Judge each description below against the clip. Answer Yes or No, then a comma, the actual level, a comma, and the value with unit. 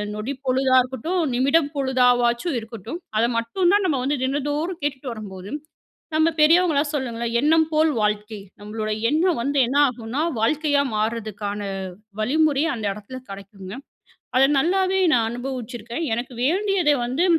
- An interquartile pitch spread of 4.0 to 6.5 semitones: Yes, average, 5.1 semitones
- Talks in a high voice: Yes, very high, 260 Hz